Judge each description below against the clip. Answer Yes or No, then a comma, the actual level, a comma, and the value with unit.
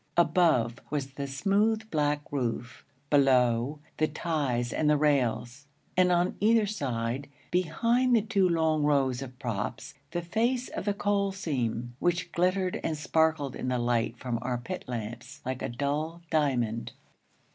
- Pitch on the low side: No, medium, 145 Hz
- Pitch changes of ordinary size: No, wide, 6.0 semitones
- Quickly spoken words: No, average, 150 wpm